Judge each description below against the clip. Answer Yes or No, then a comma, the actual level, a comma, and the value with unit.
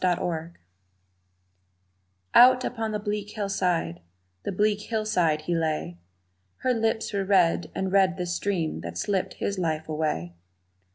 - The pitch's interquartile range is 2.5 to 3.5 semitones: No, average, 4.6 semitones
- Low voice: No, medium, 185 Hz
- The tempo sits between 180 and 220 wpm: No, slow, 135 wpm